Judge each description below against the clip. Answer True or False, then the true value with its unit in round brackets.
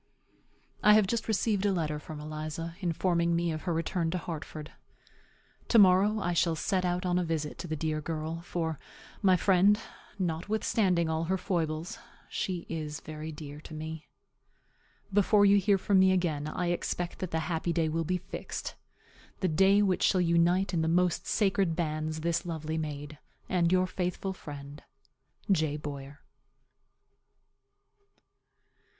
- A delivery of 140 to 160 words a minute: True (155 wpm)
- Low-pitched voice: False (170 Hz)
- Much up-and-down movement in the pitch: False (3.0 semitones)